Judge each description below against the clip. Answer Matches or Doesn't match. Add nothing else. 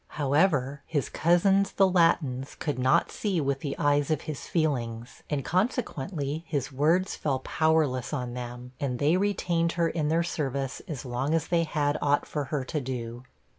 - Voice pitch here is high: Doesn't match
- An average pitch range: Matches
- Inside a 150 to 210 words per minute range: Matches